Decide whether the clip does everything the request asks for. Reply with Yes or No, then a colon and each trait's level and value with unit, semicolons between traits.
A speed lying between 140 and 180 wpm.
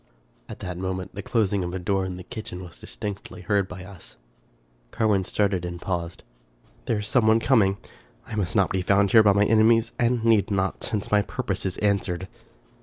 No: average, 200 wpm